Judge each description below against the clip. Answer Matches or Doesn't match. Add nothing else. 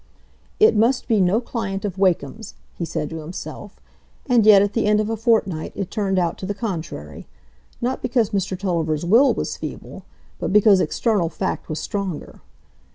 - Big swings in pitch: Doesn't match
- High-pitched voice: Matches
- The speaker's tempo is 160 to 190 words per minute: Matches